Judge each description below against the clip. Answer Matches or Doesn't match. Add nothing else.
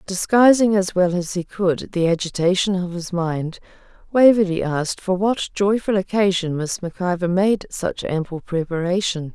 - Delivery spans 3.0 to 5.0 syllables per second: Matches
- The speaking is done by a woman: Matches